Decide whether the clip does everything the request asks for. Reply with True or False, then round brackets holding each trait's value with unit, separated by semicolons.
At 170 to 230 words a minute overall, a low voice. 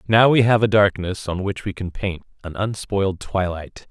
True (200 wpm; 100 Hz)